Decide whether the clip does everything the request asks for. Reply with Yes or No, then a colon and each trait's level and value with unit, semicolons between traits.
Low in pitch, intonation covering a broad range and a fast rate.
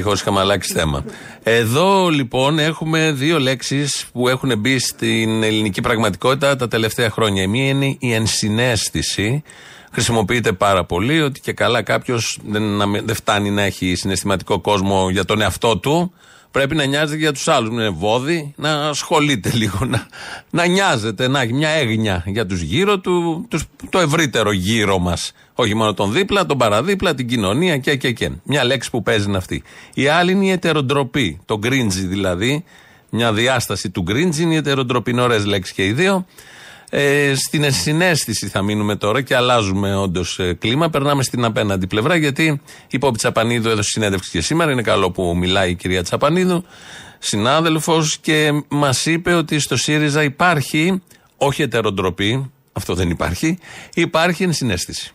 No: low, 125 Hz; wide, 6.6 semitones; average, 160 wpm